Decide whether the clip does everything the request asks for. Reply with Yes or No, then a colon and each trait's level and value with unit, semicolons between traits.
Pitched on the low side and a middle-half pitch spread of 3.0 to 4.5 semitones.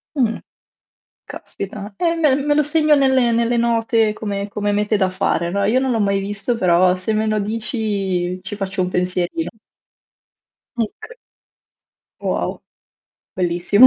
No: high, 210 Hz; average, 3.5 semitones